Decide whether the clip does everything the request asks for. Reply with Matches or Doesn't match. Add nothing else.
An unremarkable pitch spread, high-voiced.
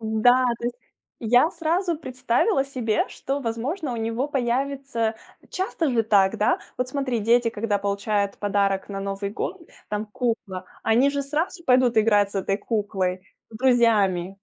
Matches